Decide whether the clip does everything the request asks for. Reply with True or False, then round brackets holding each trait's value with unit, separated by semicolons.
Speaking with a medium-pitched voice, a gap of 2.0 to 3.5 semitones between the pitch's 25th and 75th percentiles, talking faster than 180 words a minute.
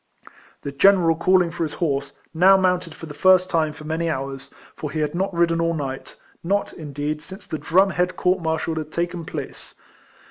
True (165 Hz; 3.0 semitones; 190 wpm)